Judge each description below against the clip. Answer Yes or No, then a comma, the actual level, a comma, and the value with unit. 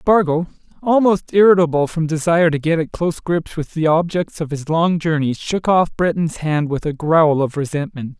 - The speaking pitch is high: No, medium, 165 Hz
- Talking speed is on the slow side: No, average, 190 wpm